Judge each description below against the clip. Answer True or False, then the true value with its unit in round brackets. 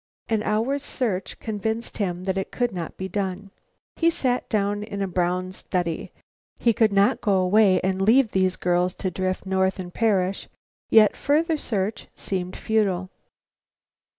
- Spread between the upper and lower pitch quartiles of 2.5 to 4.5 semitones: True (3.0 semitones)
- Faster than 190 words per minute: False (155 wpm)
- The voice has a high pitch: True (195 Hz)